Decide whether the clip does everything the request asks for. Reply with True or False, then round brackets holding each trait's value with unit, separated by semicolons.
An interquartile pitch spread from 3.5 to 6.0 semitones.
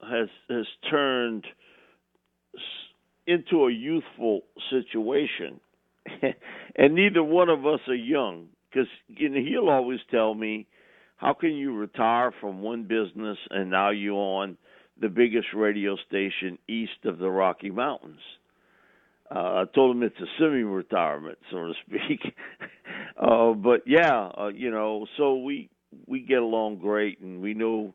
True (4.8 semitones)